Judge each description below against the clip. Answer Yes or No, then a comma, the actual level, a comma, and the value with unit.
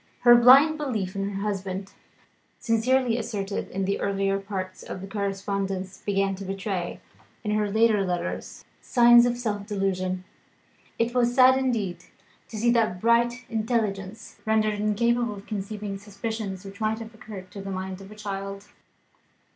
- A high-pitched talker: Yes, high, 205 Hz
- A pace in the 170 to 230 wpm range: No, average, 155 wpm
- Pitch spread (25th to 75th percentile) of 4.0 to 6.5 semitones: No, average, 2.9 semitones